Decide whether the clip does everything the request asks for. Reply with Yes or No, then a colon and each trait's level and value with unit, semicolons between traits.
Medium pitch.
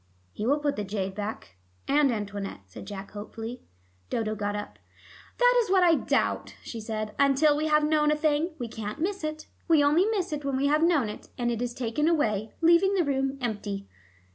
No: very high, 270 Hz